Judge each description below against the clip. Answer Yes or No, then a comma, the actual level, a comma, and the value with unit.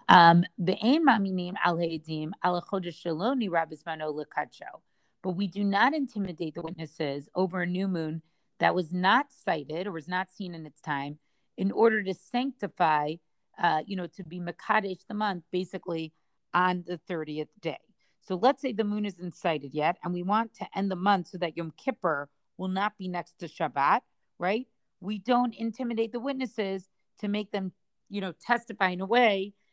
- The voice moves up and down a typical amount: Yes, average, 3.8 semitones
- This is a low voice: No, medium, 185 Hz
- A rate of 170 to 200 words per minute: No, average, 160 wpm